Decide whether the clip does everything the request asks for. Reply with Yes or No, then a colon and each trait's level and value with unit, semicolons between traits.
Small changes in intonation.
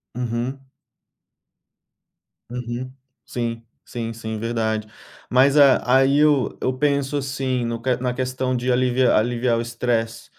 Yes: narrow, 2.1 semitones